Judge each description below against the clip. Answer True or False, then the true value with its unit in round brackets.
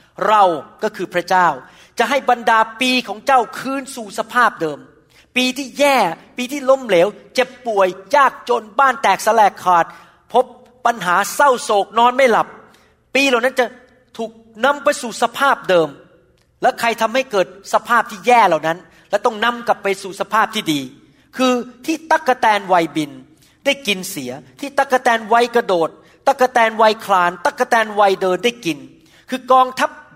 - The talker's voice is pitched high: True (230 Hz)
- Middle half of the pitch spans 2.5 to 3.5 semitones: False (5.0 semitones)